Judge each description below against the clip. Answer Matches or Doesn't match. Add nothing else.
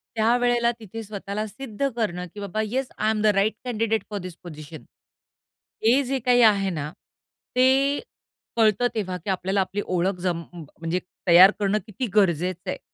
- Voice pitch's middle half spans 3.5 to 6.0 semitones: Matches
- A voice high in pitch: Matches